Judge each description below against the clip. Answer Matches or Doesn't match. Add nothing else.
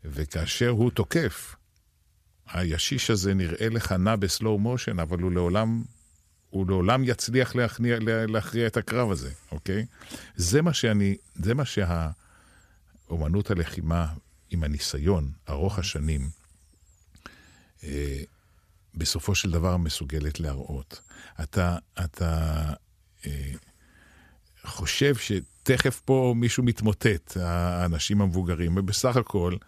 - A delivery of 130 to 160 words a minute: Doesn't match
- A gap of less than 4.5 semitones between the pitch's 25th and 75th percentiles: Doesn't match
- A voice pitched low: Matches